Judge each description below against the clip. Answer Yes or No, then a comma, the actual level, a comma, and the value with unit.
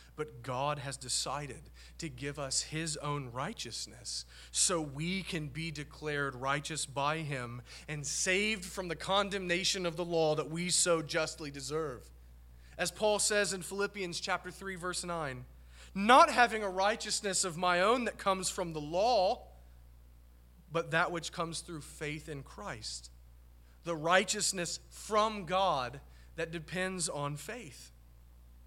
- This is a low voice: No, medium, 160 Hz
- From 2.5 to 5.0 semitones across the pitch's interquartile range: No, wide, 5.6 semitones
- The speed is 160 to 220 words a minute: No, average, 140 wpm